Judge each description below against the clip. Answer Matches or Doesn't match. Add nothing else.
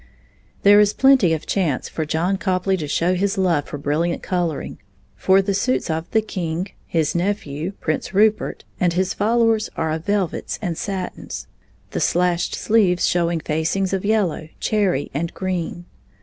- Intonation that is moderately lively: Matches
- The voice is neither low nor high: Matches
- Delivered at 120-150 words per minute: Doesn't match